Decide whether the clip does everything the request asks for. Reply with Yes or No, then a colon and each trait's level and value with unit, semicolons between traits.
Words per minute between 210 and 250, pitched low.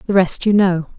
No: fast, 245 wpm; medium, 185 Hz